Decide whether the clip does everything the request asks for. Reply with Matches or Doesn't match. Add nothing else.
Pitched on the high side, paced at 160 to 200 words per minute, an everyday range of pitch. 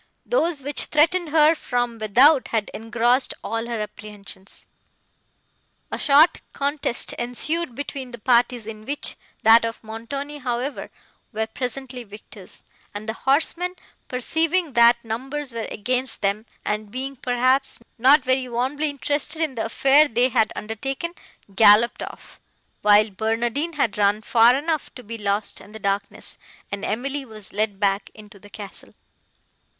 Doesn't match